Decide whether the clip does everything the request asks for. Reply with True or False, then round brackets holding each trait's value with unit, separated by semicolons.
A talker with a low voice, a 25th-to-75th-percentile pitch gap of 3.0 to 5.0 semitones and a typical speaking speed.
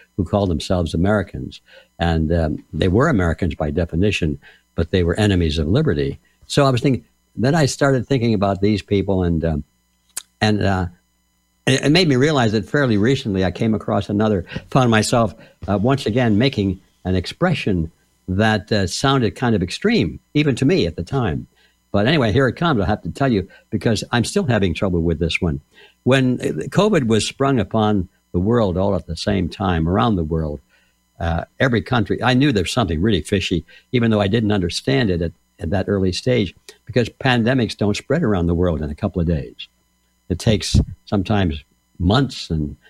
False (100 Hz; 5.5 semitones; 185 wpm)